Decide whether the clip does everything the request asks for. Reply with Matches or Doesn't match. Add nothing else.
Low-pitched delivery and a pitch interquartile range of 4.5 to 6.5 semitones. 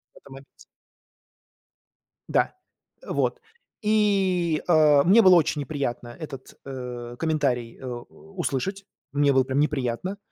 Doesn't match